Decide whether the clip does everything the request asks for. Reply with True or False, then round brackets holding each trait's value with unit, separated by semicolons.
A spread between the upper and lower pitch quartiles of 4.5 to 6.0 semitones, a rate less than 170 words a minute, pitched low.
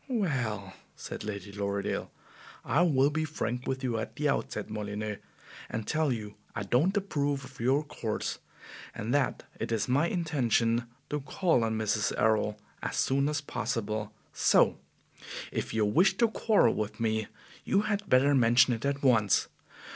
True (5.4 semitones; 160 wpm; 125 Hz)